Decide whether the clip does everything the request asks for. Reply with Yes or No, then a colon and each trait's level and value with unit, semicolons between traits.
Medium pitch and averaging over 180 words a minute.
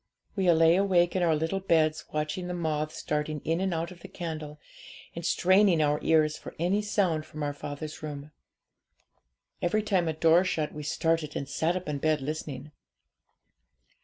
No: medium, 160 Hz; average, 175 wpm